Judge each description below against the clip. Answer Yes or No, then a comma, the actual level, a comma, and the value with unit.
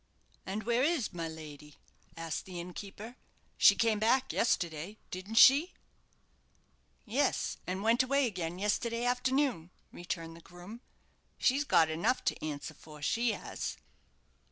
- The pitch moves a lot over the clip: Yes, wide, 6.7 semitones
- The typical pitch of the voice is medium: No, high, 205 Hz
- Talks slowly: Yes, slow, 130 wpm